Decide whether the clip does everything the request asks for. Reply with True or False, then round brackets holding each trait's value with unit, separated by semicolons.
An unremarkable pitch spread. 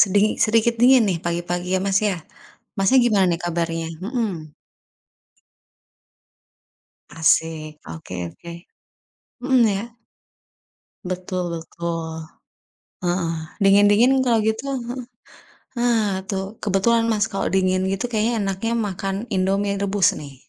True (4.3 semitones)